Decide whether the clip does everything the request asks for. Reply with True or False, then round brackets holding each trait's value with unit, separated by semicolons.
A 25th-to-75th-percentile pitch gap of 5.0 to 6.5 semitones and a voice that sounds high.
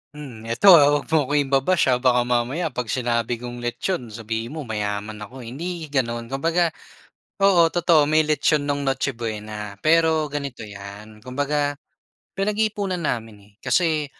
False (5.5 semitones; 135 Hz)